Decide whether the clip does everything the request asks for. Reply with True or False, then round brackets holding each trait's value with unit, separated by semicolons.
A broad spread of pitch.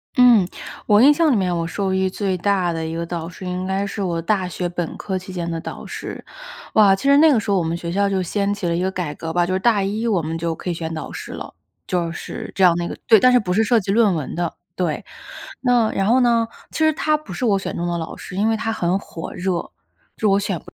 False (4.0 semitones)